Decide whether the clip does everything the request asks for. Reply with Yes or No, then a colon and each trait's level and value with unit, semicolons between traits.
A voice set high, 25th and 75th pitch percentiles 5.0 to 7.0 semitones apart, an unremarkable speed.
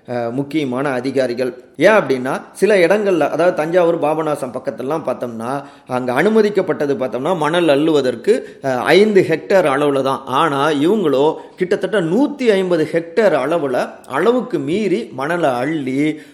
No: medium, 150 Hz; wide, 5.4 semitones; average, 115 wpm